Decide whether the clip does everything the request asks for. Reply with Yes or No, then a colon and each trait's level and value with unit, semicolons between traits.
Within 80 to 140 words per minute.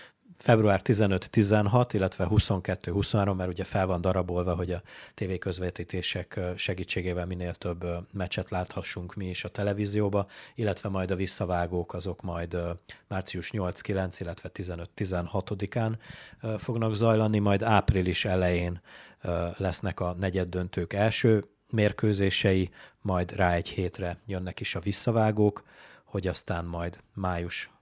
Yes: average, 120 wpm